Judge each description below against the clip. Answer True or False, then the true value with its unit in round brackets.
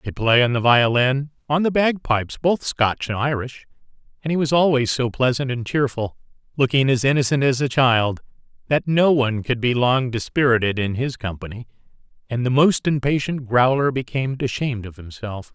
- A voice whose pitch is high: False (130 Hz)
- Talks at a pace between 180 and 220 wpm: False (170 wpm)